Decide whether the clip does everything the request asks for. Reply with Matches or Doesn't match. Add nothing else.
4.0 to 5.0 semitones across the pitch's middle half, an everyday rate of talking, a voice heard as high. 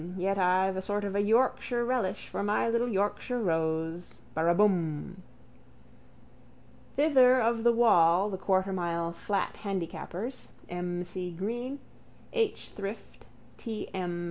Doesn't match